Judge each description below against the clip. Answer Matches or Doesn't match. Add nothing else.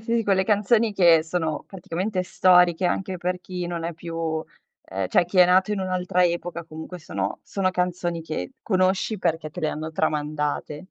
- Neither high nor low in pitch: Matches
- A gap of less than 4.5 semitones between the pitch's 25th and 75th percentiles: Matches